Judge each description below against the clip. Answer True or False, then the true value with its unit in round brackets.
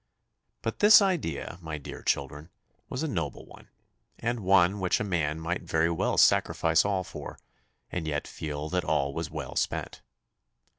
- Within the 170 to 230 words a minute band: False (160 wpm)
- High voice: False (85 Hz)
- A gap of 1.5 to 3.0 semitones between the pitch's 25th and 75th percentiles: False (4.0 semitones)